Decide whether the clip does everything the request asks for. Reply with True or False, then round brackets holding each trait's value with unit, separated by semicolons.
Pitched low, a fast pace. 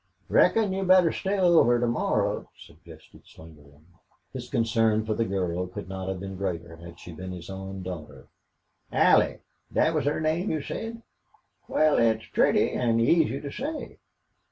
False (110 Hz; 160 wpm)